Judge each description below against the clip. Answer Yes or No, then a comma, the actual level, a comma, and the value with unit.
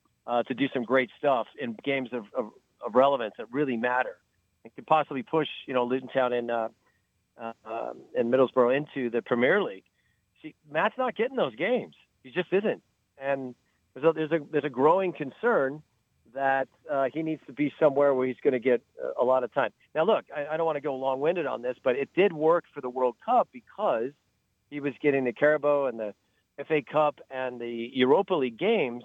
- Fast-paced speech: Yes, fast, 210 wpm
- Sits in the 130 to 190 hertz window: Yes, low, 135 Hz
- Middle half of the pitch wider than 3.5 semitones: Yes, average, 3.9 semitones